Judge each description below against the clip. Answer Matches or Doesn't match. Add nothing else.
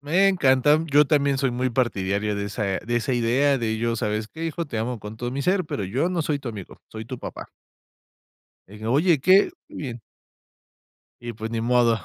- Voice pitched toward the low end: Matches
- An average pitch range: Matches